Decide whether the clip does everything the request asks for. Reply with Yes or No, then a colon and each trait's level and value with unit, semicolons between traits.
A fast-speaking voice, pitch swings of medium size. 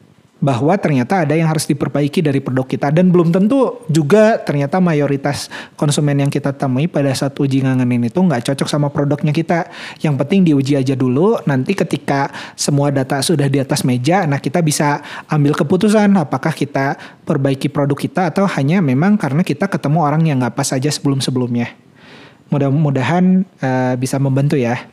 Yes: fast, 165 wpm; average, 3.6 semitones